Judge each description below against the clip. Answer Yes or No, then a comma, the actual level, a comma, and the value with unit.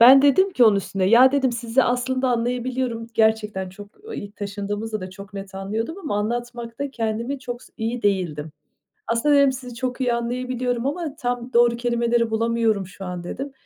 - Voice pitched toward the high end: Yes, high, 235 Hz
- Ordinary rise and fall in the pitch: Yes, average, 3.3 semitones